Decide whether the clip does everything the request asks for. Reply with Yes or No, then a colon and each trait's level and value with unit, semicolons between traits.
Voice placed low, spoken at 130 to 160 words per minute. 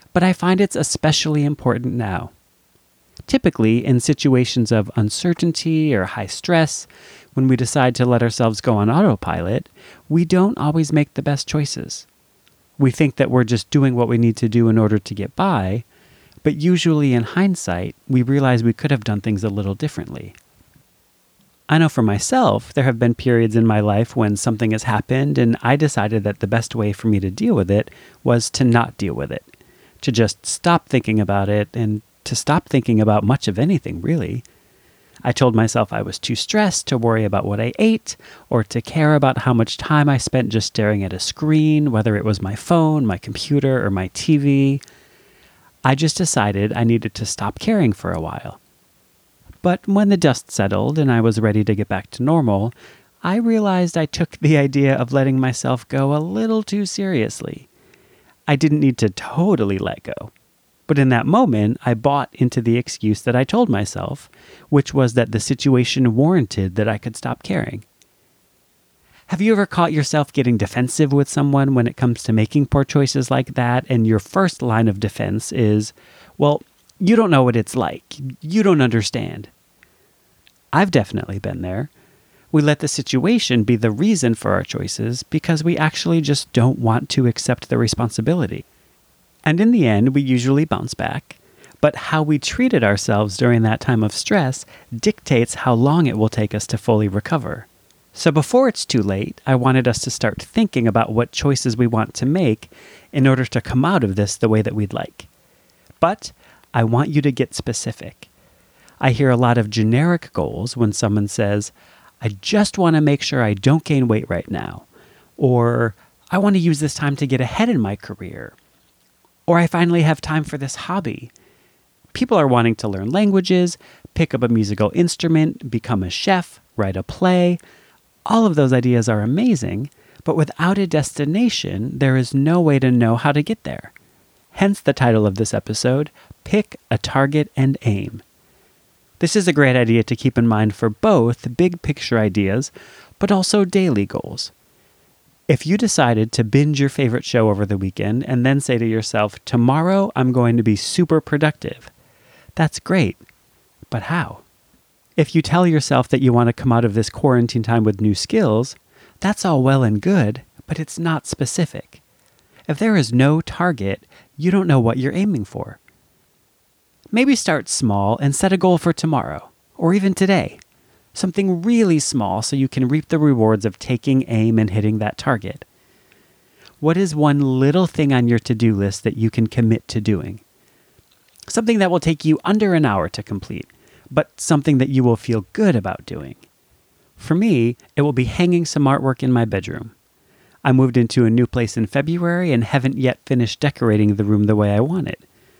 No: low, 130 Hz; average, 185 wpm